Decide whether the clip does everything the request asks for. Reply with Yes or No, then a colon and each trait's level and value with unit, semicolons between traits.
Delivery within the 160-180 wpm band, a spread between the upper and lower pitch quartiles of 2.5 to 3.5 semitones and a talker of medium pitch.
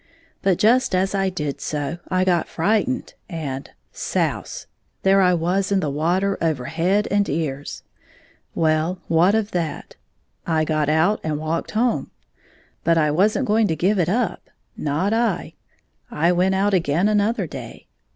No: average, 170 wpm; average, 4.3 semitones; medium, 180 Hz